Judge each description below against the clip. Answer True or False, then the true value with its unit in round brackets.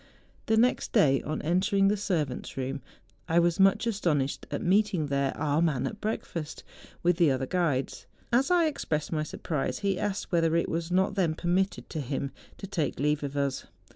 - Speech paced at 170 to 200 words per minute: True (190 wpm)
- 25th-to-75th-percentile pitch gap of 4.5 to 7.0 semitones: True (5.0 semitones)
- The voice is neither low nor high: True (170 Hz)